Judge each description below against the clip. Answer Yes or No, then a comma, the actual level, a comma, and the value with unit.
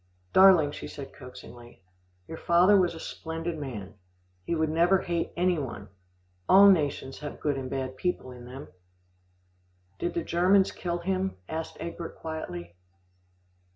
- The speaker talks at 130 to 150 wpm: Yes, average, 145 wpm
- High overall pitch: No, medium, 160 Hz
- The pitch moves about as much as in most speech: Yes, average, 4.8 semitones